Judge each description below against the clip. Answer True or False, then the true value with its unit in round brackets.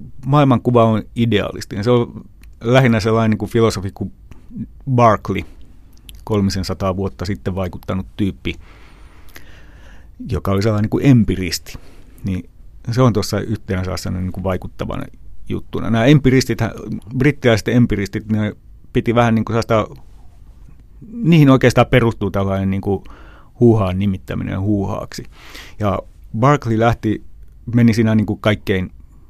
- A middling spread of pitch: True (3.8 semitones)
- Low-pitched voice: True (105 Hz)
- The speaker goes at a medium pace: True (115 wpm)